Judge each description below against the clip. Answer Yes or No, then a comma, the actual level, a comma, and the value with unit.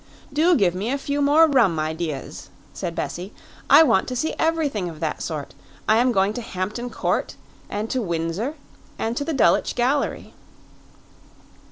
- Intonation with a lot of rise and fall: Yes, wide, 8.2 semitones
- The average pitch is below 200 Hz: No, high, 225 Hz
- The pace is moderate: Yes, average, 165 wpm